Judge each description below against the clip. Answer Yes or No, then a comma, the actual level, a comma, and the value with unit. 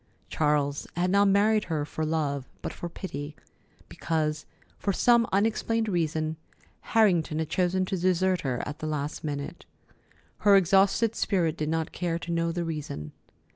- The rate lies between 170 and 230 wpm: No, average, 155 wpm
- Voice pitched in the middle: Yes, medium, 165 Hz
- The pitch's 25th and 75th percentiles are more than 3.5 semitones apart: Yes, average, 3.9 semitones